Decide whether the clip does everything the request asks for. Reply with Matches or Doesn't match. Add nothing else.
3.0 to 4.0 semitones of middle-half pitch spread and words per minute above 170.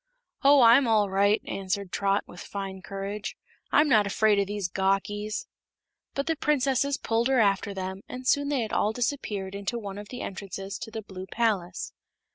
Matches